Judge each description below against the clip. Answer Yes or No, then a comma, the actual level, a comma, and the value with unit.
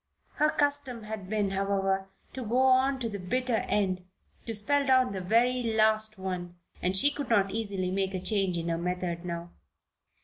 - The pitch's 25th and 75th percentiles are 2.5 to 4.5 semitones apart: No, average, 4.9 semitones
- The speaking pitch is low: No, high, 205 Hz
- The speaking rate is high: No, average, 180 wpm